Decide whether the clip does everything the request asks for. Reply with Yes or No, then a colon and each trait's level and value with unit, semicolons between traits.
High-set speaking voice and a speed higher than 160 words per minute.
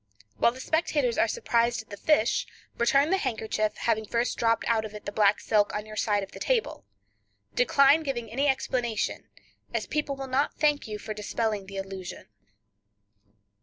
Yes: high, 230 Hz; average, 175 wpm